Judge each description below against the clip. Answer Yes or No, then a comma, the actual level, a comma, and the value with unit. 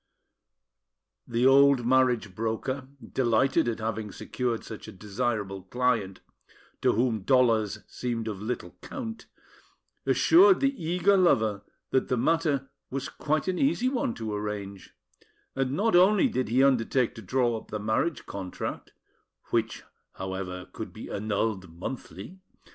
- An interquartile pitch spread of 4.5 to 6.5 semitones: Yes, average, 4.8 semitones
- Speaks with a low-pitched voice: Yes, low, 120 Hz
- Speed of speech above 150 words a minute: No, slow, 135 wpm